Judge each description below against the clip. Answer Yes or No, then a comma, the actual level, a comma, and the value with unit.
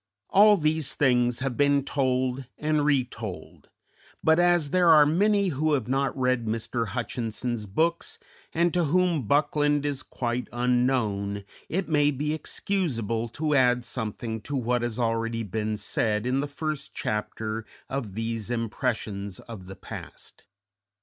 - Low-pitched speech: Yes, low, 125 Hz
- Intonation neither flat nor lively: Yes, average, 4.6 semitones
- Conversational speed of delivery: Yes, average, 145 wpm